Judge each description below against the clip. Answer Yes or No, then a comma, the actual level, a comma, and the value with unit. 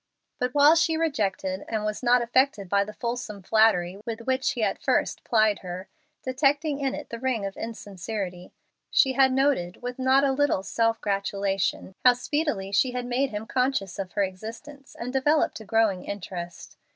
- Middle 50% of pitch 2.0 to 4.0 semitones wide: No, average, 5.0 semitones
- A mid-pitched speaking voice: No, high, 230 Hz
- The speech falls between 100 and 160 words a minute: No, average, 175 wpm